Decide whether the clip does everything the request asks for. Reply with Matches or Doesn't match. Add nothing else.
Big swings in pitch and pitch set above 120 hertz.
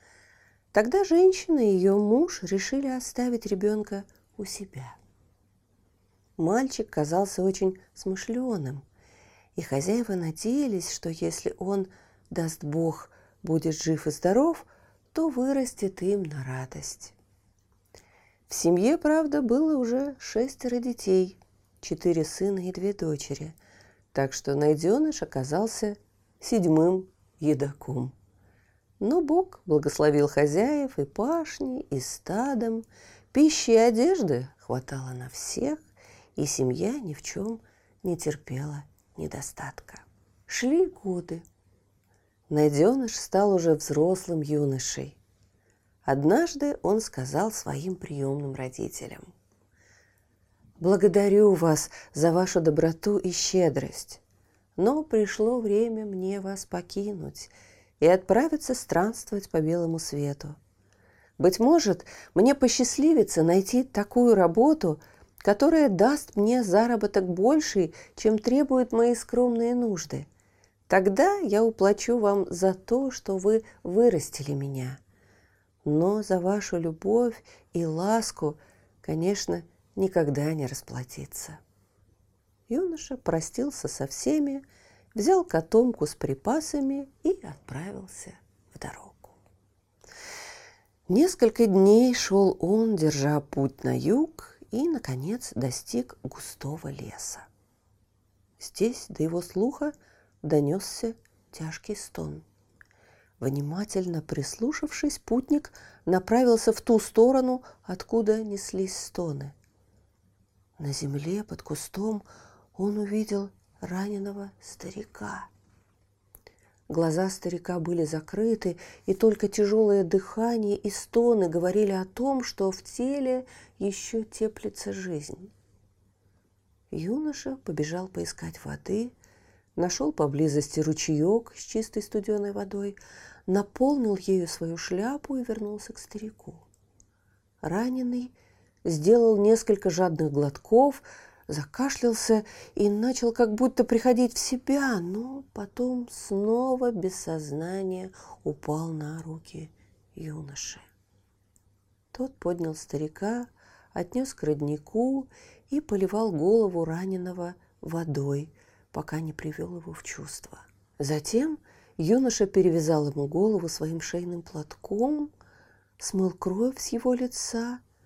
Matches